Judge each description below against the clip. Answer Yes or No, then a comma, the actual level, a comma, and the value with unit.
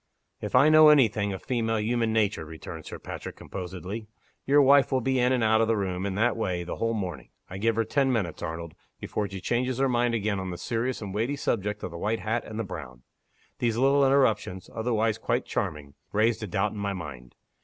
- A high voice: No, low, 110 Hz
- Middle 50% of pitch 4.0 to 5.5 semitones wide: Yes, average, 4.3 semitones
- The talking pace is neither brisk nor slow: No, fast, 225 wpm